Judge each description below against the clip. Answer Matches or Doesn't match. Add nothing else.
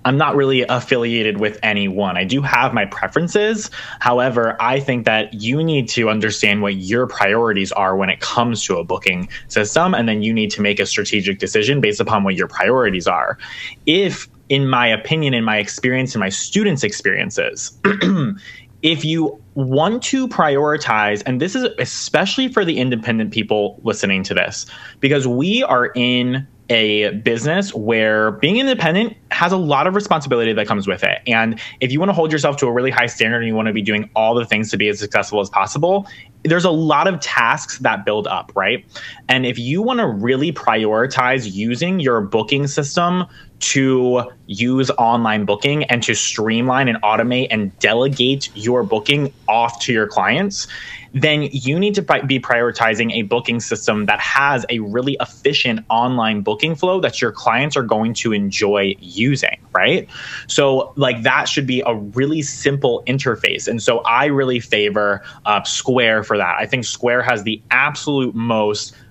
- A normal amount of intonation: Matches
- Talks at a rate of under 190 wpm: Matches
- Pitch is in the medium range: Doesn't match